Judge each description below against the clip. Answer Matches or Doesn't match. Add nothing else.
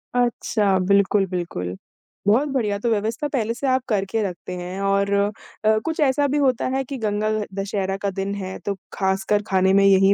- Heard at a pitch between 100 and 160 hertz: Doesn't match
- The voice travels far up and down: Doesn't match